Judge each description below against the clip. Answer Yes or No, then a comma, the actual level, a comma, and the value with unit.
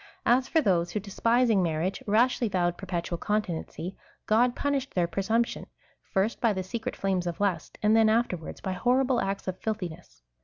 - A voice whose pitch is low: No, high, 200 Hz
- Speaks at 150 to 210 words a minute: Yes, average, 185 wpm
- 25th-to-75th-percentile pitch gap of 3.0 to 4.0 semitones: No, average, 4.6 semitones